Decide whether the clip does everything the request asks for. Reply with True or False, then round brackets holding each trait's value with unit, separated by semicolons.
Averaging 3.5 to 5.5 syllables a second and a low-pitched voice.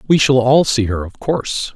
True (5.1 syllables/s; 125 Hz)